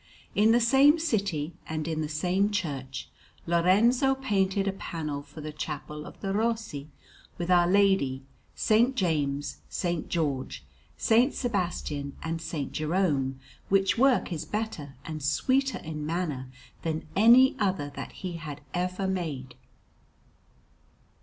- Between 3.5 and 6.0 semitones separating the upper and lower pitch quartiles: Yes, average, 5.2 semitones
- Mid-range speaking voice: Yes, medium, 175 Hz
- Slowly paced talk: Yes, slow, 130 wpm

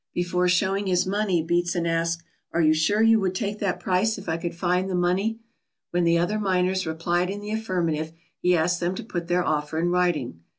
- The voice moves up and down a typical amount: No, narrow, 2.1 semitones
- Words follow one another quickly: Yes, fast, 210 wpm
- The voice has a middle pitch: Yes, medium, 180 Hz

